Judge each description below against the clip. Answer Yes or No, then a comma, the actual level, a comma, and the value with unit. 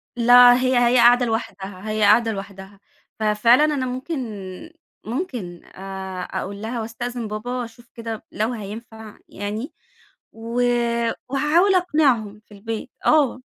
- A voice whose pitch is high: Yes, high, 230 Hz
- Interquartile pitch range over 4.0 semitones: No, average, 3.0 semitones